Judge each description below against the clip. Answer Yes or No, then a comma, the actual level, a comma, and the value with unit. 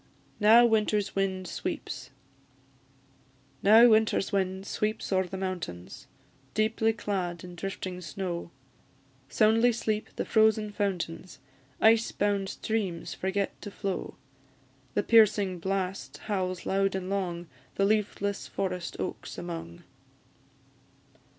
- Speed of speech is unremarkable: No, slow, 110 wpm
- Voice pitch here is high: Yes, high, 195 Hz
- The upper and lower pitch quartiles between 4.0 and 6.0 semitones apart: No, average, 2.7 semitones